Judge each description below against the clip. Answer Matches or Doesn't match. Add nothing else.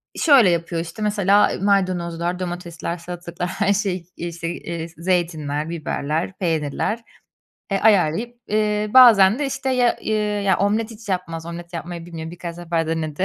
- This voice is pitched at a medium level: Matches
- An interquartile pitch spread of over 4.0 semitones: Doesn't match